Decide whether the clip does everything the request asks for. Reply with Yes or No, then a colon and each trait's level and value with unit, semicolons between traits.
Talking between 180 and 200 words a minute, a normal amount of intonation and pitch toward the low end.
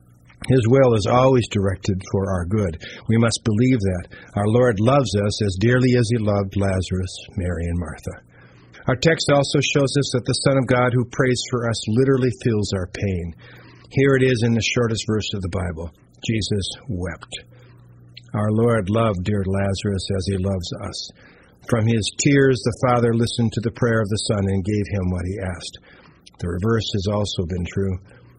Yes: average, 185 wpm; average, 4.2 semitones; low, 110 Hz